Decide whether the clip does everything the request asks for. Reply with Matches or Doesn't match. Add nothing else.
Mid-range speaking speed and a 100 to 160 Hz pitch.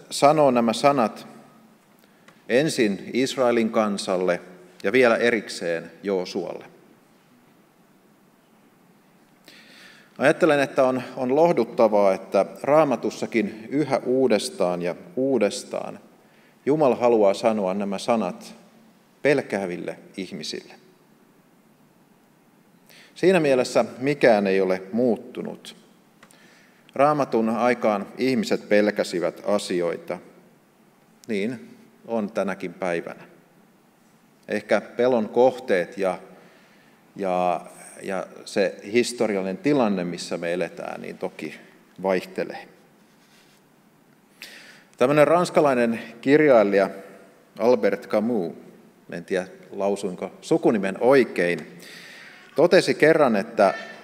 Doesn't match